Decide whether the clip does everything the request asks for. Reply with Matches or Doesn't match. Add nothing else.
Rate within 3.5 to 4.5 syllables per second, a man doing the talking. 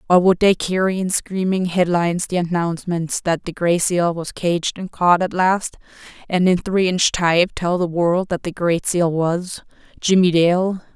Doesn't match